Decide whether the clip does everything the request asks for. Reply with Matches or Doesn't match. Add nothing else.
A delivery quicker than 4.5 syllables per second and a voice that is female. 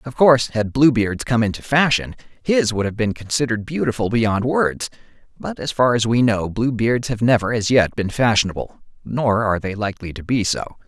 Doesn't match